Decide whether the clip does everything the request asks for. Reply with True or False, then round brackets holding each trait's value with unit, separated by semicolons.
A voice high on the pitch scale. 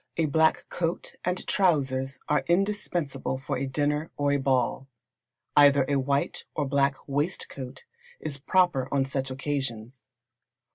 False (140 Hz)